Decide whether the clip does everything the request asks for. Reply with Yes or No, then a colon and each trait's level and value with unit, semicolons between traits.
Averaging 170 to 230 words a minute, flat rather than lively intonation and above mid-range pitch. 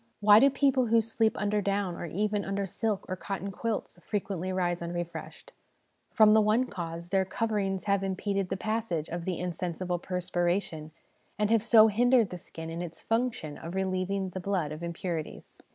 No: average, 180 wpm; average, 3.4 semitones; high, 195 Hz